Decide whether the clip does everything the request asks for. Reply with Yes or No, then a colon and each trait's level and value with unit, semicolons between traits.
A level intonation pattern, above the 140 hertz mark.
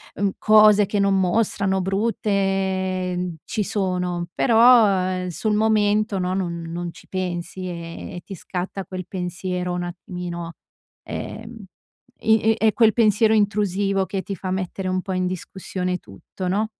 Yes: narrow, 2.3 semitones; high, 190 Hz